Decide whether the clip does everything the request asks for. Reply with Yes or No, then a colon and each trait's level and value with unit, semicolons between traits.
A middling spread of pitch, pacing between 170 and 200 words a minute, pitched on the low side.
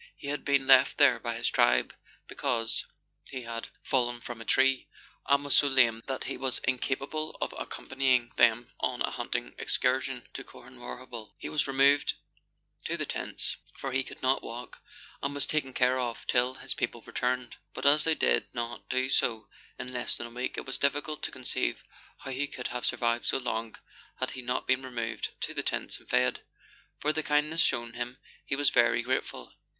No: narrow, 2.3 semitones; average, 190 wpm; low, 130 Hz